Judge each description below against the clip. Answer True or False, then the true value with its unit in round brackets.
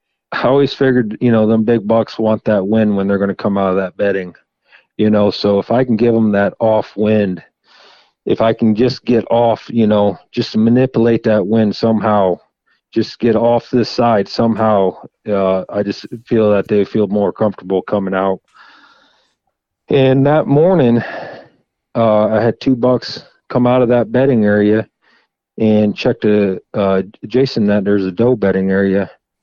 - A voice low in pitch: True (110 Hz)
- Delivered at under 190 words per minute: True (175 wpm)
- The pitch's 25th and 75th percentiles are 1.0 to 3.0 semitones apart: True (2.6 semitones)